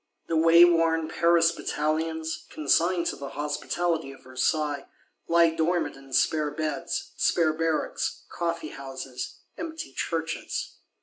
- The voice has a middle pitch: Yes, medium, 160 Hz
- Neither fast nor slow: No, slow, 110 wpm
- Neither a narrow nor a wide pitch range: No, narrow, 2.1 semitones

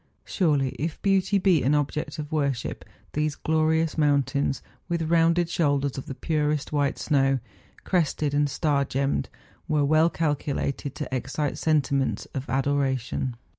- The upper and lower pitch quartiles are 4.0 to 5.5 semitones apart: No, narrow, 2.4 semitones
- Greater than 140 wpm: No, slow, 135 wpm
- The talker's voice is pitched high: No, medium, 150 Hz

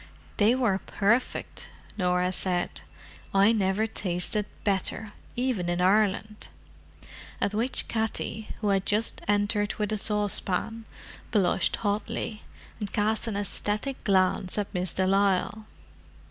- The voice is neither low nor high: No, high, 205 Hz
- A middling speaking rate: No, slow, 120 wpm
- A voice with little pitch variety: Yes, narrow, 2.2 semitones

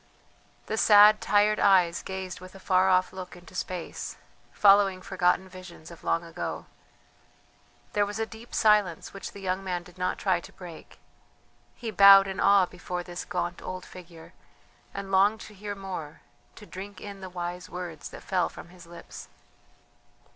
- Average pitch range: No, narrow, 2.0 semitones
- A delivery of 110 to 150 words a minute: No, average, 170 wpm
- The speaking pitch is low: No, medium, 185 Hz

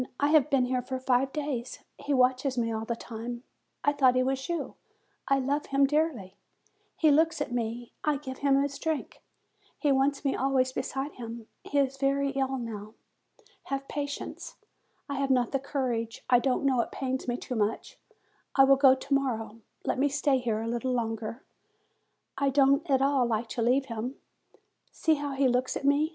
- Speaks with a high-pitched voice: Yes, very high, 265 Hz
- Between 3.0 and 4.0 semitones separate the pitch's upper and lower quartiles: No, narrow, 2.4 semitones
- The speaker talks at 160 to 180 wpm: No, average, 190 wpm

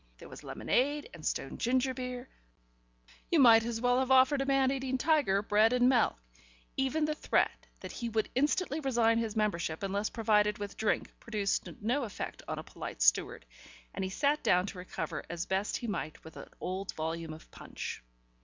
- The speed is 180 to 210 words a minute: Yes, average, 185 wpm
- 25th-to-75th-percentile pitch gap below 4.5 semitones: No, average, 4.9 semitones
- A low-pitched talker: No, high, 230 Hz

